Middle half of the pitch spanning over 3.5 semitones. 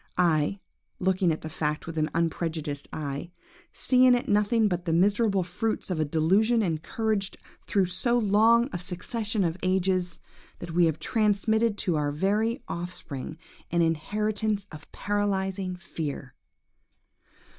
Yes: average, 4.5 semitones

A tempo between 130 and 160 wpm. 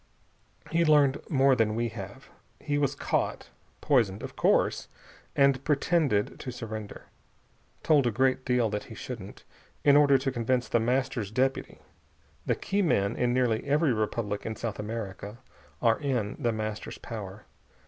Yes: average, 150 wpm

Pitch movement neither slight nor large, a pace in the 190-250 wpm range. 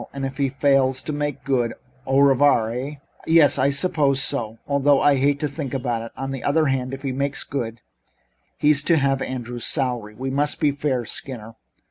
No: narrow, 2.0 semitones; average, 195 wpm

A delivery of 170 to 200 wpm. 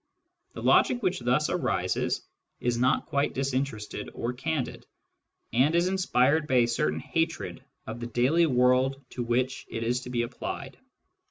No: average, 155 wpm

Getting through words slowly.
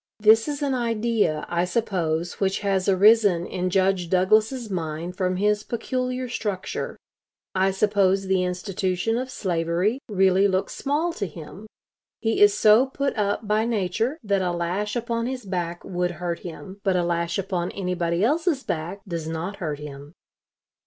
No: average, 160 wpm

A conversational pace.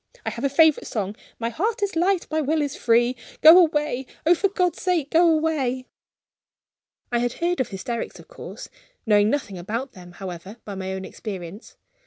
Yes: average, 185 wpm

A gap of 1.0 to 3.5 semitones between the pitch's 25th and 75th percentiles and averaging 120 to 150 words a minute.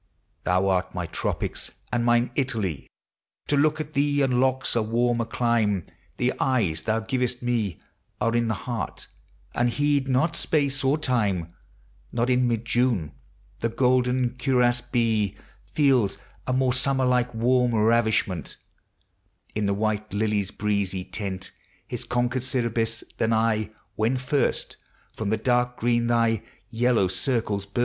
Yes: average, 3.0 semitones; average, 140 wpm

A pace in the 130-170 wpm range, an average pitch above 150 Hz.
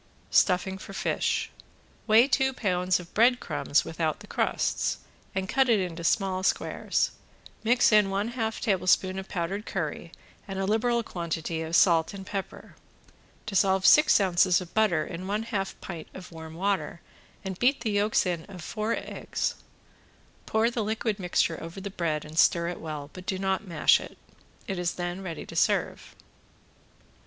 Yes: average, 165 wpm; high, 190 Hz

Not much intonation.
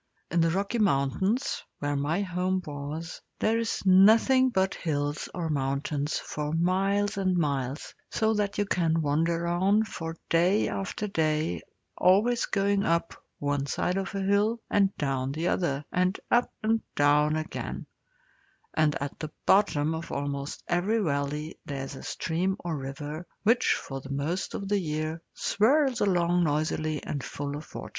No: average, 5.1 semitones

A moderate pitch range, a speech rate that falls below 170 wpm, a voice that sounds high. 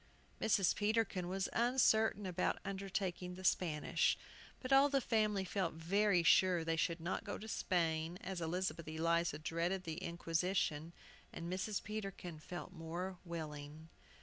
No: average, 3.1 semitones; average, 140 wpm; medium, 180 Hz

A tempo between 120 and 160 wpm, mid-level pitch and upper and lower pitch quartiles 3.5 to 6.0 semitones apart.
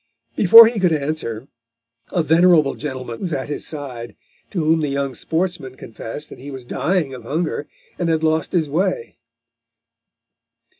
Yes: average, 155 wpm; medium, 155 Hz; average, 4.2 semitones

